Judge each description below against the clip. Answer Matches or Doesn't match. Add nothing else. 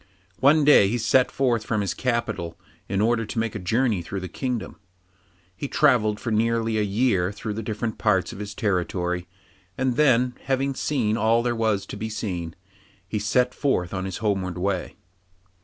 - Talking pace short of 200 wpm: Matches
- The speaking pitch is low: Matches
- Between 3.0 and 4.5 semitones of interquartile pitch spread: Matches